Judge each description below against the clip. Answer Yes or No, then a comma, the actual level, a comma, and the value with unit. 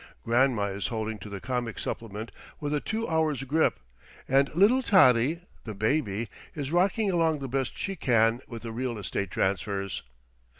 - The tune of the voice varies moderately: No, wide, 6.2 semitones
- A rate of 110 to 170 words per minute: Yes, average, 165 wpm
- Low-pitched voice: Yes, low, 125 Hz